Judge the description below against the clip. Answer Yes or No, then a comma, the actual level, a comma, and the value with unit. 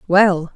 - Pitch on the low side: No, medium, 185 Hz